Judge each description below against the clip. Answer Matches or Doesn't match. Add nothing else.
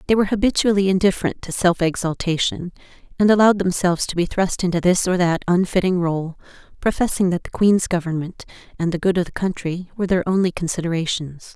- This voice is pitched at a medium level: Matches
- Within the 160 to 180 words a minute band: Matches